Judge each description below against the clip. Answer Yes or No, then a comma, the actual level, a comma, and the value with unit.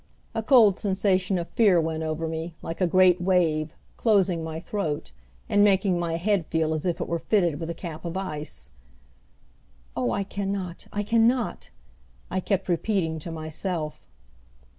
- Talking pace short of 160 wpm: No, average, 170 wpm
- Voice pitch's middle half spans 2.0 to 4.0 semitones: Yes, average, 3.5 semitones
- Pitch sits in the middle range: Yes, medium, 175 Hz